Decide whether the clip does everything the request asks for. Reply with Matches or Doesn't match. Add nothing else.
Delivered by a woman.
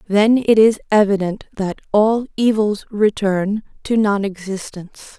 Matches